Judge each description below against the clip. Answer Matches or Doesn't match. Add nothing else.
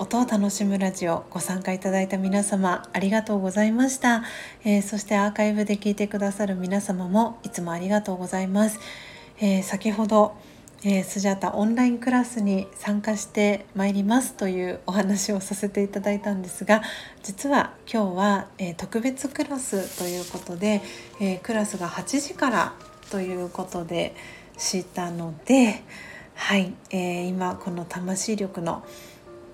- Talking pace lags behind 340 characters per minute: Matches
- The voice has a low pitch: Doesn't match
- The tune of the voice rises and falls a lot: Doesn't match